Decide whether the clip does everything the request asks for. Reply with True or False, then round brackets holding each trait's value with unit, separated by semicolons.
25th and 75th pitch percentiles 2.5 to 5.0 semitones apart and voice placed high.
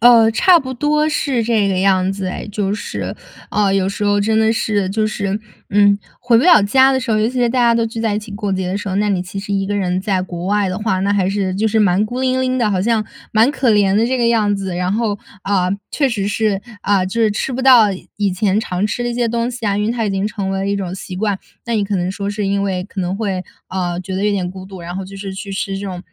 True (2.8 semitones; 205 Hz)